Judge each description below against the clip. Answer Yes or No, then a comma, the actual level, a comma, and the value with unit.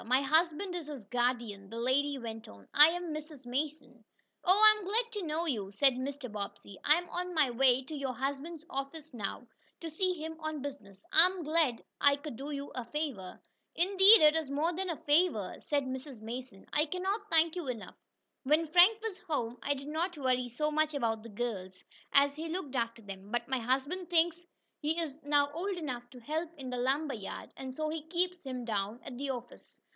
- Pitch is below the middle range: No, very high, 285 Hz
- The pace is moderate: No, fast, 210 wpm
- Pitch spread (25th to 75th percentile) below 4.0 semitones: No, average, 4.8 semitones